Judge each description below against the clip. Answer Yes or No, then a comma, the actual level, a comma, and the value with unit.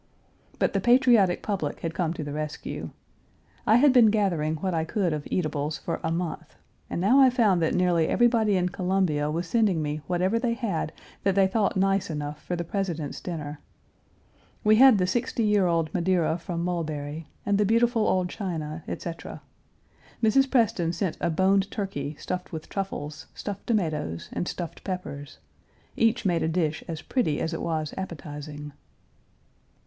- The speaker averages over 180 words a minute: No, average, 170 wpm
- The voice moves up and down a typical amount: Yes, average, 4.5 semitones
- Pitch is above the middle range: No, medium, 180 Hz